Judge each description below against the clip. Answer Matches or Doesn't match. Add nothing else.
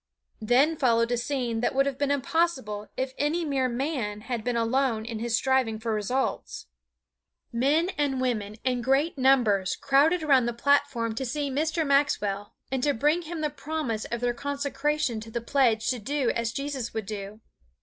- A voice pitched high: Matches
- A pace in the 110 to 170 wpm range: Doesn't match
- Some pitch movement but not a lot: Matches